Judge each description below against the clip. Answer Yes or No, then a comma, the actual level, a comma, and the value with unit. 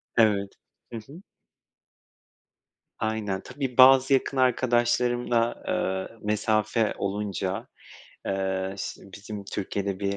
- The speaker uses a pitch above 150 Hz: No, low, 110 Hz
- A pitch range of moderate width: Yes, average, 3.6 semitones